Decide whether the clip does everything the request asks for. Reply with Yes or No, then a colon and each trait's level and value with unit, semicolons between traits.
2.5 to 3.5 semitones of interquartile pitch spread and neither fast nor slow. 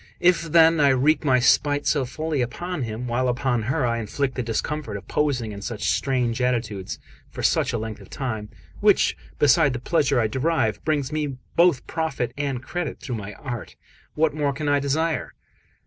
No: average, 4.2 semitones; average, 185 wpm